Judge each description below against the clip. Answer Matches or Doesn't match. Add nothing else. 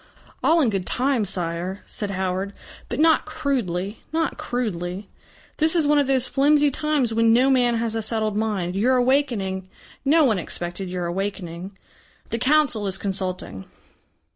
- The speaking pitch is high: Matches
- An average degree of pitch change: Doesn't match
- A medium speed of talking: Matches